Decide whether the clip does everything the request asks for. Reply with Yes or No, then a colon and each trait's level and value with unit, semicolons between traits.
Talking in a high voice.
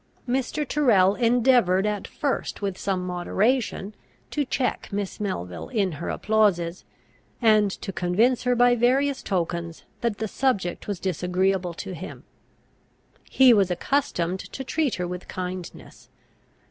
Yes: high, 200 Hz